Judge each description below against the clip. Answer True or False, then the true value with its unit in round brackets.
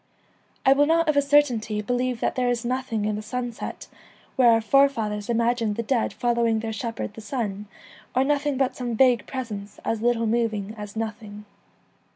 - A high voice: True (235 Hz)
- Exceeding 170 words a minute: True (185 wpm)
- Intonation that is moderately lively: True (3.0 semitones)